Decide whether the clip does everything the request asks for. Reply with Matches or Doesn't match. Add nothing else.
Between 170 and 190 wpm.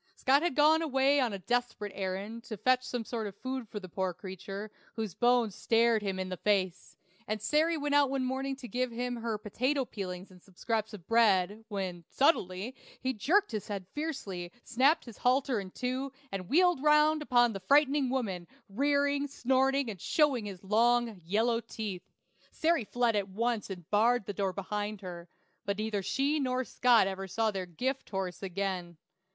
Matches